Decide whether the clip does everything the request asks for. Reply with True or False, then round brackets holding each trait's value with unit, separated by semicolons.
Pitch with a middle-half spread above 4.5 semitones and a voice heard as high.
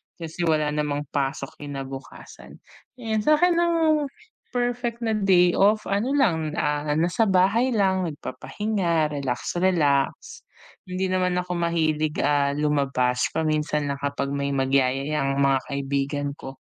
False (5.6 semitones; 155 Hz)